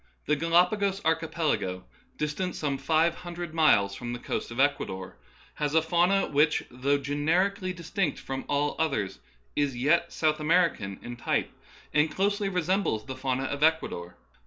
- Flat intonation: No, average, 4.3 semitones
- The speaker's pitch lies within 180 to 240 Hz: No, medium, 150 Hz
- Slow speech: No, average, 160 wpm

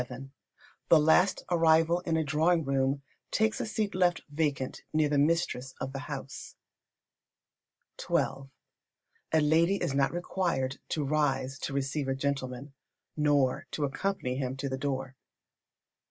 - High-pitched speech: No, medium, 145 Hz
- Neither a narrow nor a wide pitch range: Yes, average, 3.3 semitones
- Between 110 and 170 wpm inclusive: Yes, average, 140 wpm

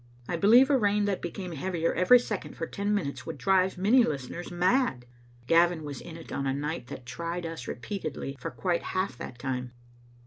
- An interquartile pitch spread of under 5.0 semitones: No, wide, 5.6 semitones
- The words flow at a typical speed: Yes, average, 195 wpm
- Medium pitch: Yes, medium, 170 Hz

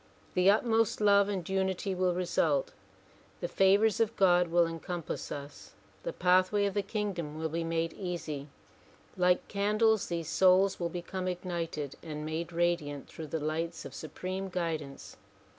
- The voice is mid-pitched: Yes, medium, 180 Hz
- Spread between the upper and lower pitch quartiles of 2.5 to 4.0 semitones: Yes, average, 2.9 semitones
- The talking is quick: No, average, 150 wpm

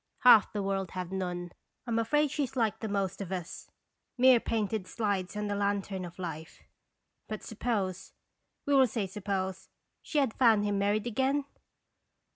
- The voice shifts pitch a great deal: No, average, 3.4 semitones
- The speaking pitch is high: Yes, high, 205 Hz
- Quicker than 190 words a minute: No, average, 170 wpm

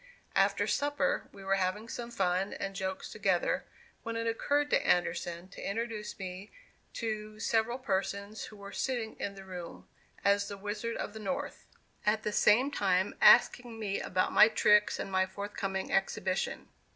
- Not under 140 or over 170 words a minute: Yes, average, 165 wpm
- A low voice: No, high, 205 Hz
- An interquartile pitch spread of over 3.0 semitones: No, average, 2.7 semitones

